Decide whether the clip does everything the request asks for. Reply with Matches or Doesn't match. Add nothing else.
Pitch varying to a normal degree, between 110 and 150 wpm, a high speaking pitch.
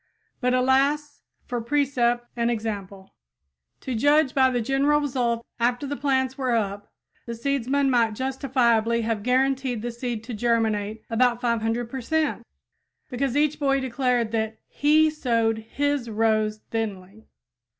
Matches